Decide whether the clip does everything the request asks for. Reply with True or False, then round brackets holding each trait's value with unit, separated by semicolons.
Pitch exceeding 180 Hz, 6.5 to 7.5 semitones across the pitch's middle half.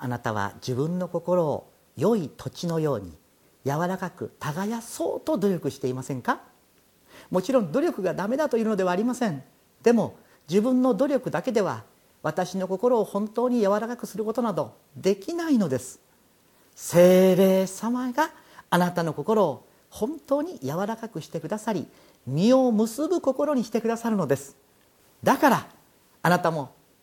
True (190 Hz; 7.1 semitones)